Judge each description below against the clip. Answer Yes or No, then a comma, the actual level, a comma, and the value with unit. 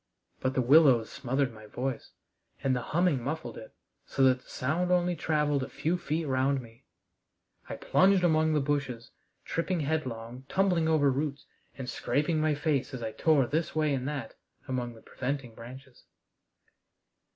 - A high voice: No, medium, 140 Hz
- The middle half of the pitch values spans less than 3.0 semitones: No, average, 3.7 semitones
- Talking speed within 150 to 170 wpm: Yes, average, 160 wpm